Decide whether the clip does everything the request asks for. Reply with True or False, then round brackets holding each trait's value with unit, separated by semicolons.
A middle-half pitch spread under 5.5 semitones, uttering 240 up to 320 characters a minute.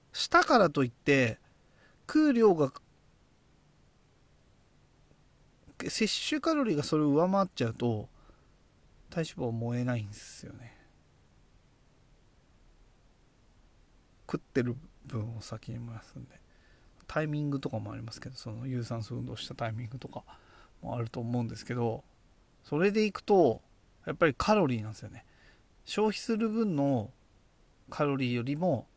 True (5.1 semitones; 260 characters per minute)